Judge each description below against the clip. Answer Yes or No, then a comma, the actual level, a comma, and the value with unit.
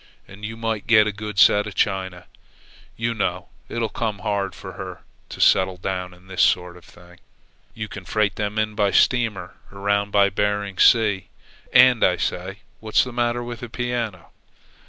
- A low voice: Yes, low, 105 Hz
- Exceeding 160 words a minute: Yes, average, 175 wpm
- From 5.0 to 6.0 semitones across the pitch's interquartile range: No, average, 2.9 semitones